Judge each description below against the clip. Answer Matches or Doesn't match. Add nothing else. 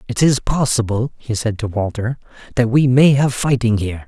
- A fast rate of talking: Doesn't match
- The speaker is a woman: Doesn't match